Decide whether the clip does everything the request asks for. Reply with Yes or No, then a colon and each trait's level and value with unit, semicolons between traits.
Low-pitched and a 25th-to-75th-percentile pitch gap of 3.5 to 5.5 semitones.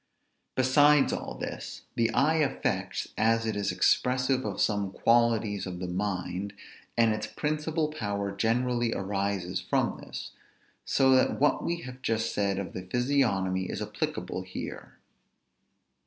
Yes: low, 115 Hz; average, 4.8 semitones